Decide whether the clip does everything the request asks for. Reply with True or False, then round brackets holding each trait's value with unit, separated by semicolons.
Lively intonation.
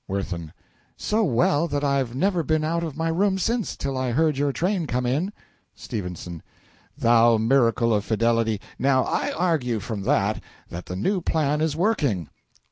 True (6.0 semitones)